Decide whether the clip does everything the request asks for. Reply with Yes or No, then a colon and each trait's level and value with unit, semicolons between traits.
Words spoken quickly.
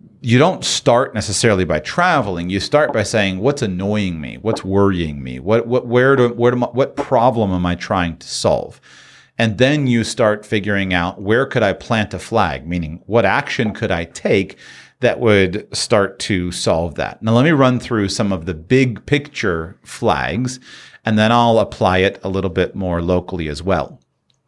No: average, 190 wpm